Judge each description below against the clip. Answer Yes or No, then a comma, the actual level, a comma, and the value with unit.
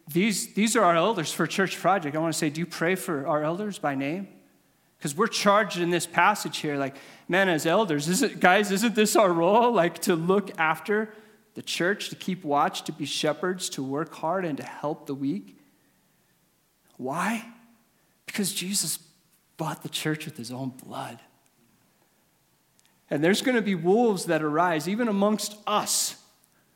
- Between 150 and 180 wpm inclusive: Yes, average, 175 wpm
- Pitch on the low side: No, medium, 175 Hz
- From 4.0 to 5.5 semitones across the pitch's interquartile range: Yes, average, 4.6 semitones